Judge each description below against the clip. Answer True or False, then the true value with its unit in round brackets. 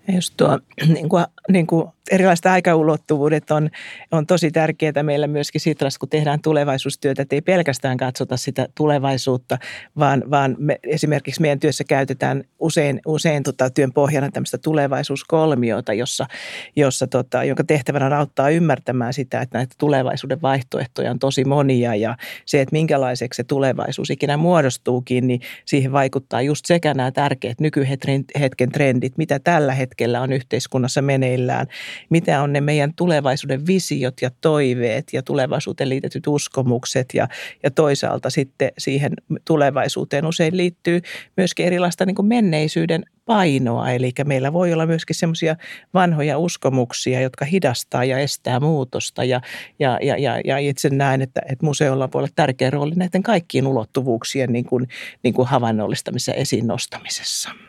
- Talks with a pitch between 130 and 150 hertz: True (140 Hz)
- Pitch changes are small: False (3.1 semitones)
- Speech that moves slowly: False (140 wpm)